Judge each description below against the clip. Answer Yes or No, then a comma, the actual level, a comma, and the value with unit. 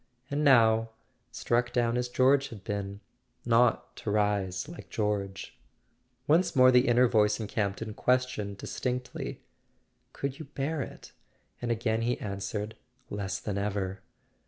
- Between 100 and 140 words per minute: Yes, slow, 135 wpm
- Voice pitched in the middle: No, low, 115 Hz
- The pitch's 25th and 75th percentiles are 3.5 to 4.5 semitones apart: Yes, average, 3.8 semitones